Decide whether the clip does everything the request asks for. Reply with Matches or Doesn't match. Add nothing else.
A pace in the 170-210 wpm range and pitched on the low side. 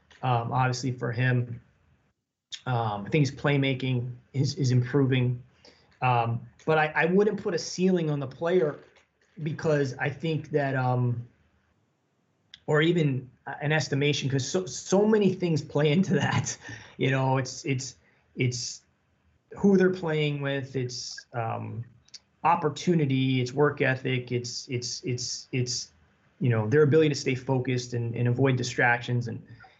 Doesn't match